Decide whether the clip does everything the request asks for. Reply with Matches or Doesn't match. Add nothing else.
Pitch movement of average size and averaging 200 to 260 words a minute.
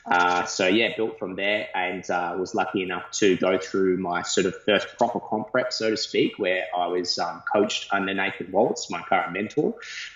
Matches